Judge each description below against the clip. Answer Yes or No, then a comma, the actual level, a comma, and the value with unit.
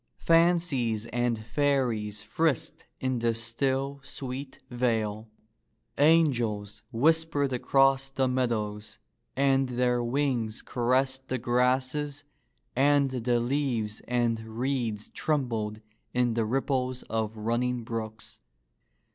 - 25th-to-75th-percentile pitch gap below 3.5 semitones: Yes, average, 3.1 semitones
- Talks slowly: Yes, slow, 105 wpm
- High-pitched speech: No, low, 125 Hz